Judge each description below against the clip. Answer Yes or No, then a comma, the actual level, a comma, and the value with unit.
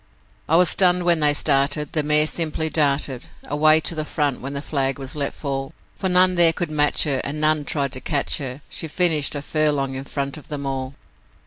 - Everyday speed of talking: No, fast, 215 wpm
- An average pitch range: No, narrow, 2.3 semitones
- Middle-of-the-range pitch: Yes, medium, 150 Hz